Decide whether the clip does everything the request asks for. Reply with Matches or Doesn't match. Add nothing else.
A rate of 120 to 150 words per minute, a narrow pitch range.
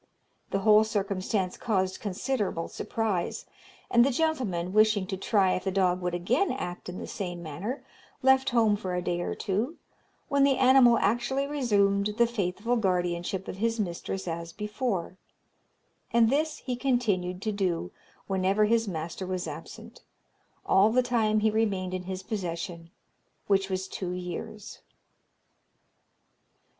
Doesn't match